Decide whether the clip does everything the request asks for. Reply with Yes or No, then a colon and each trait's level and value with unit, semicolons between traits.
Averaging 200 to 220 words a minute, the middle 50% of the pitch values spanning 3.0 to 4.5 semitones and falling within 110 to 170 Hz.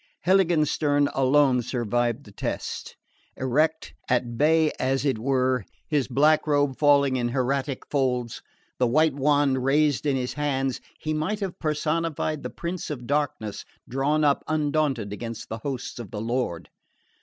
No: average, 145 wpm; average, 3.4 semitones; medium, 140 Hz